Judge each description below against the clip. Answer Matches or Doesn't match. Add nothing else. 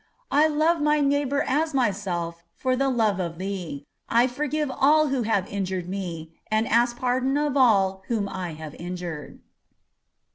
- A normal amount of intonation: Doesn't match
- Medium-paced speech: Matches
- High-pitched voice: Matches